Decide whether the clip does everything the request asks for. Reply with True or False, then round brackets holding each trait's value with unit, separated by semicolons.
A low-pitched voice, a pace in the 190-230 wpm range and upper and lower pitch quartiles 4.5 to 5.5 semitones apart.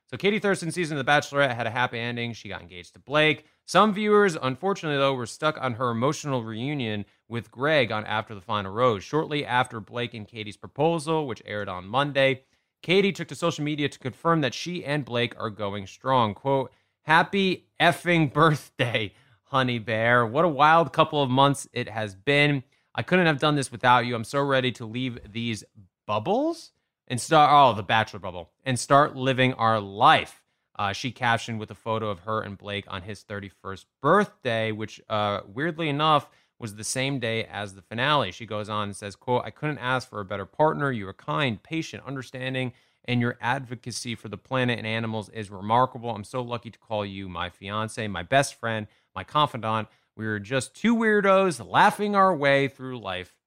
True (125 Hz; 195 wpm; 5.0 semitones)